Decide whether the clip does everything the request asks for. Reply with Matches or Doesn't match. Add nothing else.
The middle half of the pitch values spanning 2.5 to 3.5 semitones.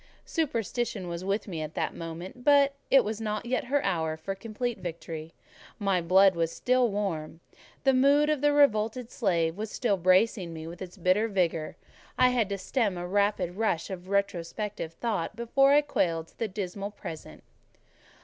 Doesn't match